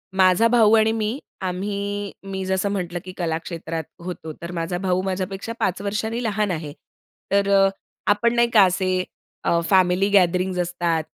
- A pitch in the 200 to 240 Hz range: No, high, 190 Hz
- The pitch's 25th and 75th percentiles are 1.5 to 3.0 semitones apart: Yes, narrow, 2.4 semitones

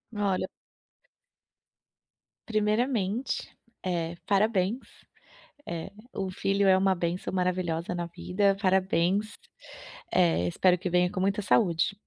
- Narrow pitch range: Yes, narrow, 2.3 semitones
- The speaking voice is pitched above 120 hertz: Yes, medium, 185 Hz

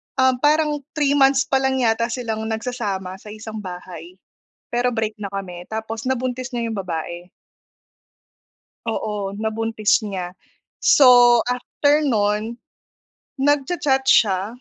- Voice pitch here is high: Yes, high, 225 Hz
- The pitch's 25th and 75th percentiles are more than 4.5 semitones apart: No, average, 4.2 semitones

